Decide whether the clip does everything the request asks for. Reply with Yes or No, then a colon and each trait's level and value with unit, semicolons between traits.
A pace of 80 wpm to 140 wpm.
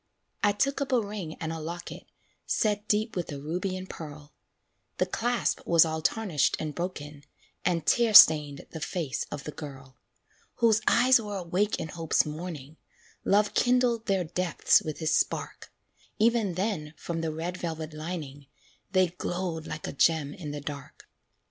No: average, 165 wpm